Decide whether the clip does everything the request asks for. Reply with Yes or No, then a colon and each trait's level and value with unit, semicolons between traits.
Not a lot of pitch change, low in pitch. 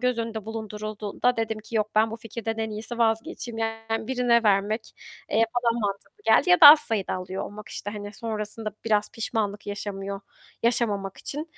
No: narrow, 1.9 semitones; high, 220 Hz